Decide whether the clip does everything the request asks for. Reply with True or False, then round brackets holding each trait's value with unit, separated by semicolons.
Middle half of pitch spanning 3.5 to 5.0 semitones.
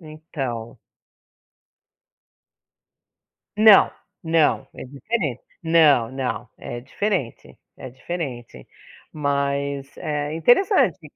True (4.0 semitones)